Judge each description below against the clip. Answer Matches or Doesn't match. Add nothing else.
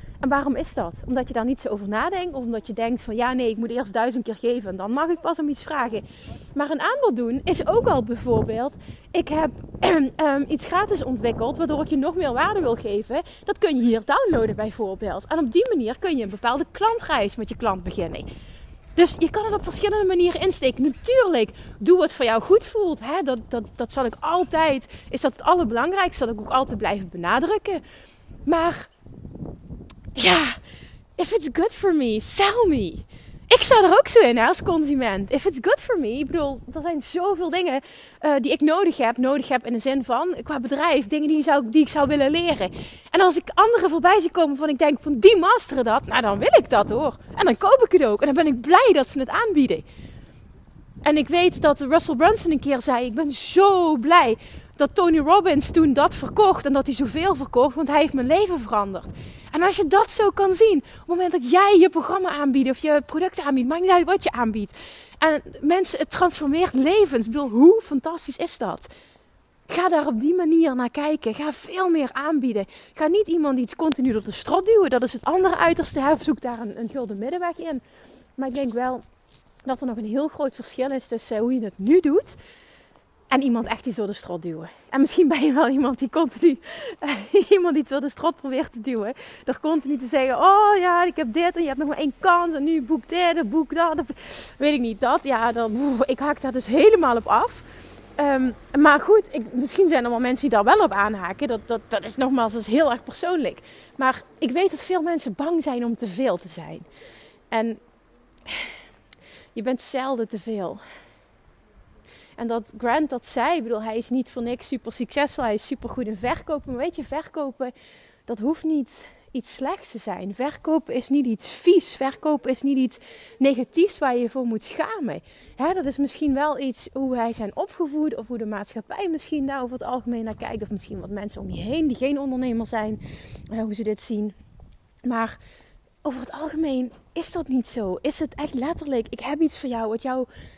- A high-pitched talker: Matches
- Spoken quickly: Matches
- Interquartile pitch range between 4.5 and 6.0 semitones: Matches